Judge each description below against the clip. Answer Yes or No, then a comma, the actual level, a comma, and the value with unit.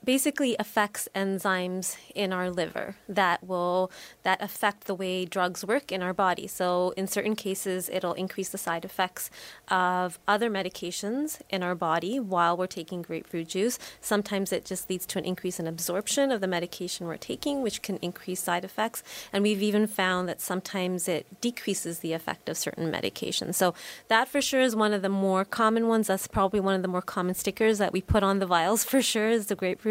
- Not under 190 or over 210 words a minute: Yes, average, 200 wpm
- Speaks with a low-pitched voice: No, high, 190 Hz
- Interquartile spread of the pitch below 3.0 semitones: Yes, narrow, 2.5 semitones